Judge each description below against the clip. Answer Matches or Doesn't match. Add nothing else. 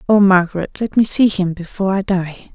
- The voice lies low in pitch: Doesn't match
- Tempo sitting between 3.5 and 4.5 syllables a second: Doesn't match